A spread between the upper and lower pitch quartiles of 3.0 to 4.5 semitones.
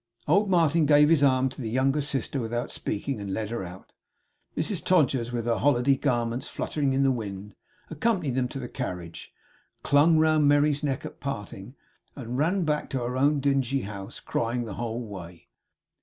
Yes: average, 4.0 semitones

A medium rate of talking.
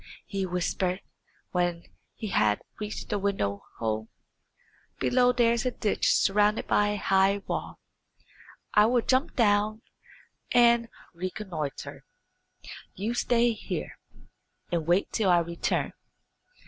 No: slow, 120 wpm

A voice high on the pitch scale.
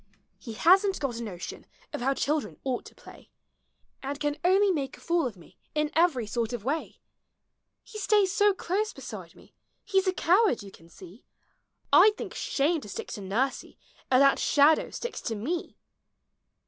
Yes: very high, 290 Hz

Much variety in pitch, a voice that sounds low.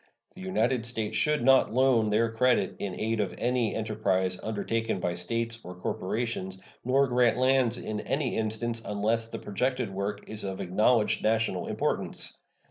No: average, 3.0 semitones; low, 115 Hz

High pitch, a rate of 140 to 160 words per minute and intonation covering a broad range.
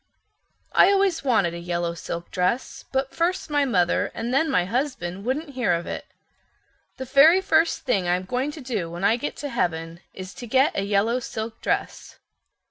No: high, 235 Hz; average, 185 wpm; wide, 7.5 semitones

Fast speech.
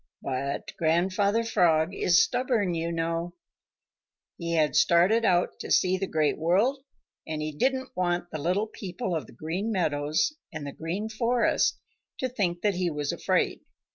No: average, 160 wpm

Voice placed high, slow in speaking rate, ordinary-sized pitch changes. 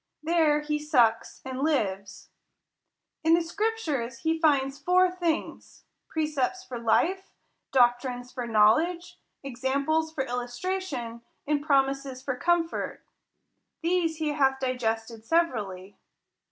Yes: very high, 280 Hz; slow, 110 wpm; average, 4.9 semitones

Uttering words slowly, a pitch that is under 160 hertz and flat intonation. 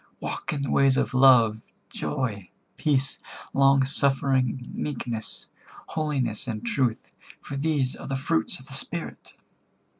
Yes: slow, 130 wpm; low, 135 Hz; narrow, 2.3 semitones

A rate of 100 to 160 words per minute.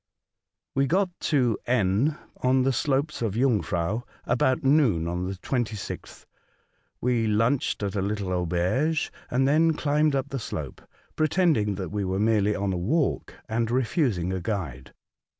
Yes: average, 150 wpm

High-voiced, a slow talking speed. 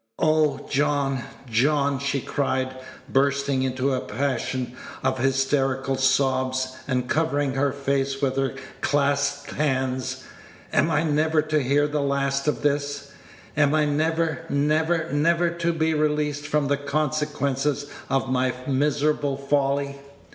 No: medium, 140 Hz; slow, 130 wpm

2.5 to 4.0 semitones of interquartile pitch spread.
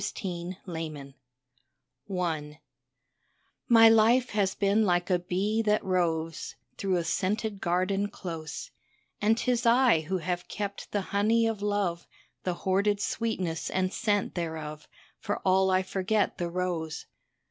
Yes: average, 3.3 semitones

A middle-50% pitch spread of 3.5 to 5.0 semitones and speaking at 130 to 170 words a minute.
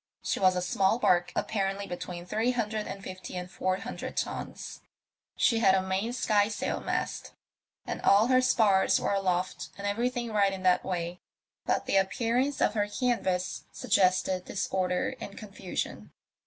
No: average, 3.0 semitones; average, 160 wpm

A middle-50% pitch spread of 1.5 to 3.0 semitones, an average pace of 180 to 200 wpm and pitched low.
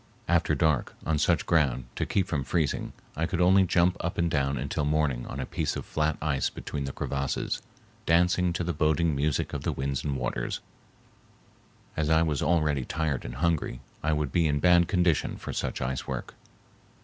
No: average, 3.5 semitones; average, 195 wpm; very low, 75 Hz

